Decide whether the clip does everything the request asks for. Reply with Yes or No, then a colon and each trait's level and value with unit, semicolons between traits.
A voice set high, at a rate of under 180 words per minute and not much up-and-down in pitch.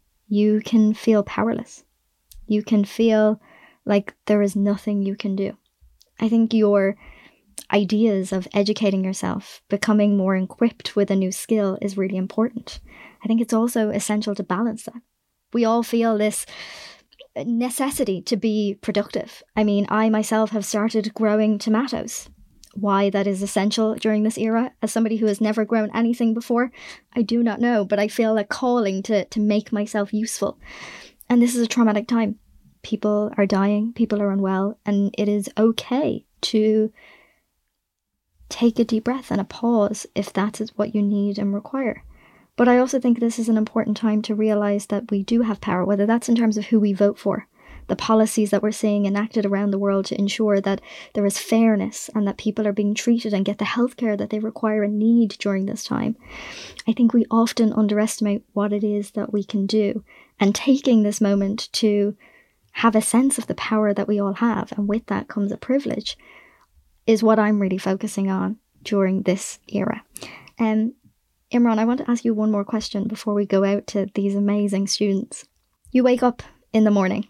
No: high, 215 Hz; average, 185 wpm; narrow, 2.0 semitones